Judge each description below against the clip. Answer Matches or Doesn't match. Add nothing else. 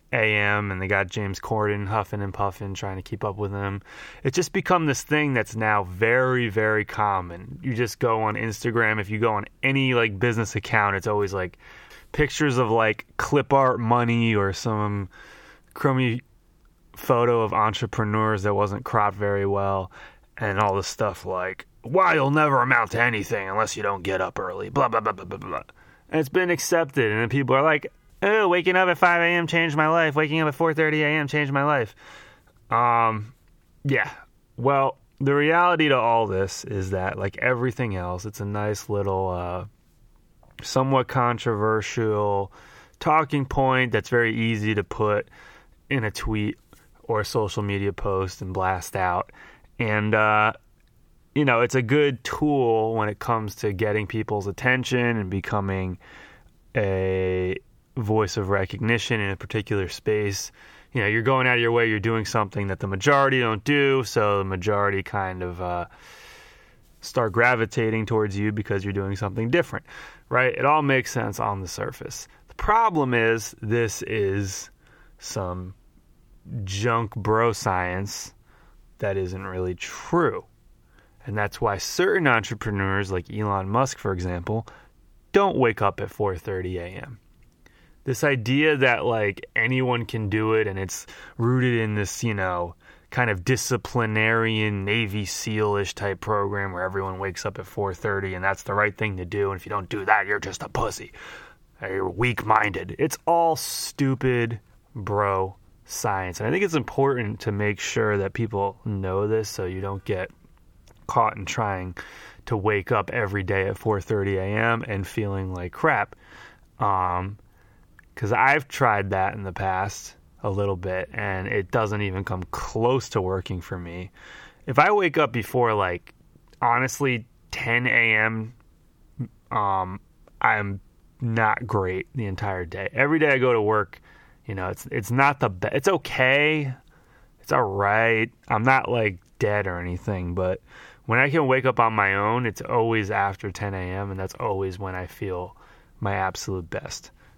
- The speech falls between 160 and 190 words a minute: Matches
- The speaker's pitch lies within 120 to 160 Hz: Doesn't match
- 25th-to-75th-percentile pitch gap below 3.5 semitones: Doesn't match